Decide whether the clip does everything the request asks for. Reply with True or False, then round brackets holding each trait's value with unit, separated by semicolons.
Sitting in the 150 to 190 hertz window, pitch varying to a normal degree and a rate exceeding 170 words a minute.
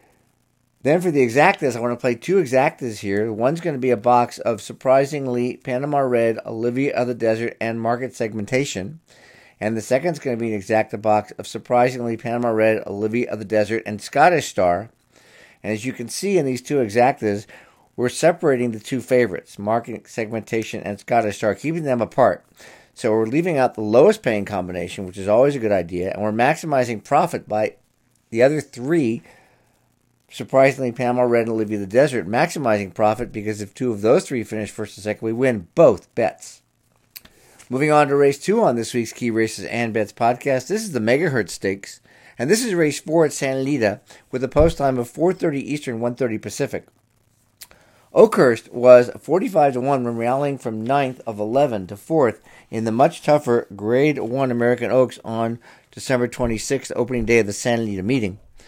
False (120 Hz; 3.2 semitones; 190 wpm)